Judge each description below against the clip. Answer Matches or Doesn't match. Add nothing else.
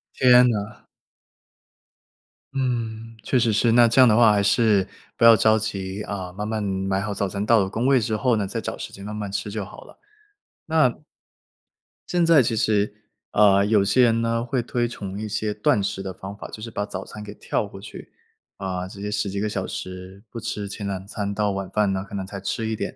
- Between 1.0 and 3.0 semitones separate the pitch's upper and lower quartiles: Matches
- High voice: Doesn't match